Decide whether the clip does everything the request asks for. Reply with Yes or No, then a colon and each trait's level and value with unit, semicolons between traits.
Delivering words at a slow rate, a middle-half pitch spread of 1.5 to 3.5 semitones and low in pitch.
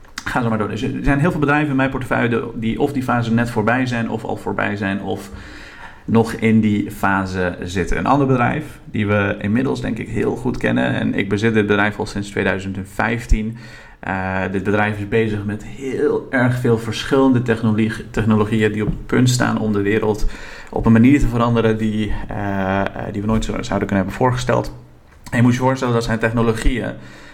No: fast, 200 wpm; average, 2.8 semitones; low, 110 Hz